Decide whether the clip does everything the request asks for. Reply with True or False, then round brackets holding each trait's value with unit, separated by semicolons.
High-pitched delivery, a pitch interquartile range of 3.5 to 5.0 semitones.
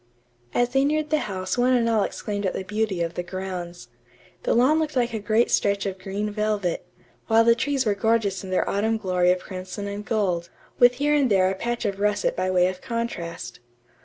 True (205 Hz; 4.0 semitones)